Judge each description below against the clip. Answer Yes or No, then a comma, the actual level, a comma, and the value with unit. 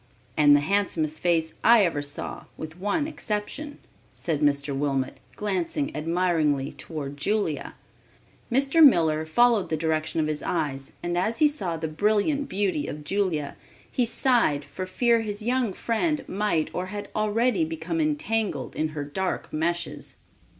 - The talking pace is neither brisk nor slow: Yes, average, 150 wpm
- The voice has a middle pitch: Yes, medium, 175 Hz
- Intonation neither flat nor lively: No, wide, 5.8 semitones